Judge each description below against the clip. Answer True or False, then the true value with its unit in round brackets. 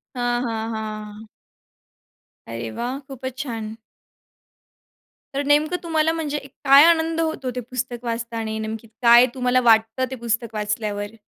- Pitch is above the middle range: True (240 Hz)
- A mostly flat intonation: False (3.6 semitones)